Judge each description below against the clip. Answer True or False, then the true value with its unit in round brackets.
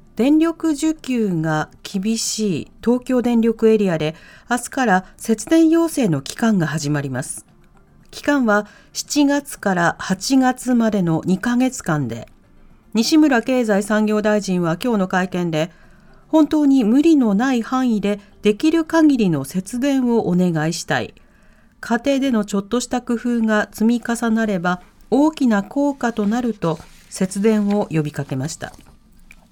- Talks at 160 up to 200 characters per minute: False (265 characters per minute)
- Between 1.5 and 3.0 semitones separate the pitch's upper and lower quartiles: False (5.4 semitones)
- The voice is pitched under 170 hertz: False (220 Hz)